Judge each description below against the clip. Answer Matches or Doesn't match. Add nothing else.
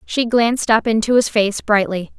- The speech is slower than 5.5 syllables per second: Matches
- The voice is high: Matches